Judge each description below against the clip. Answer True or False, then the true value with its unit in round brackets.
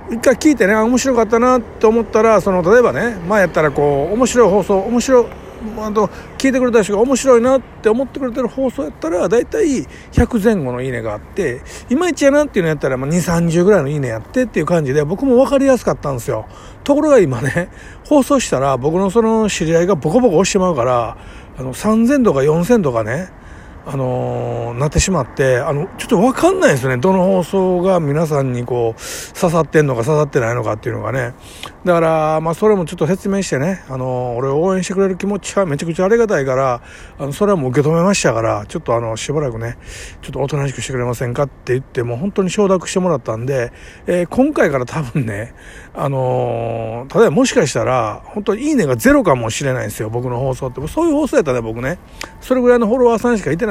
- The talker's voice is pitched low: False (175 Hz)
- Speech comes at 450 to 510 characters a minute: True (455 characters per minute)